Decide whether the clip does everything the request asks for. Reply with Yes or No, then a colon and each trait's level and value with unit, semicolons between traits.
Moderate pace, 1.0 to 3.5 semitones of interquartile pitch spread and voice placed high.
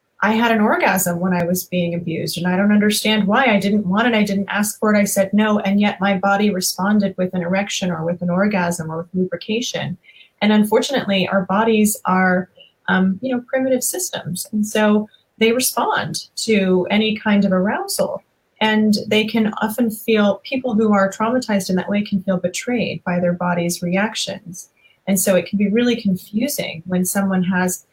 Yes: average, 190 wpm; average, 2.9 semitones; high, 200 Hz